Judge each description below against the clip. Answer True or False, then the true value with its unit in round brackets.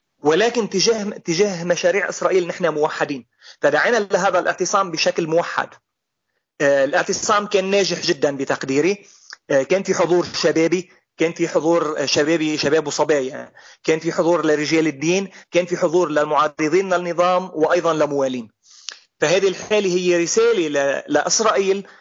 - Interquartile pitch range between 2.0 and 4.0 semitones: True (3.5 semitones)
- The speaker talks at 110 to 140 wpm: True (125 wpm)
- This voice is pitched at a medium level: True (175 Hz)